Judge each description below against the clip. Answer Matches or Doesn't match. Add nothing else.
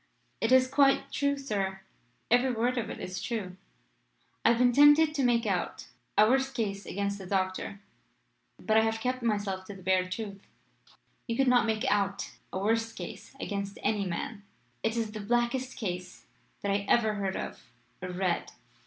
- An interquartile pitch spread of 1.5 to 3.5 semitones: Doesn't match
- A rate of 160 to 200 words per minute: Matches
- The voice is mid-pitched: Doesn't match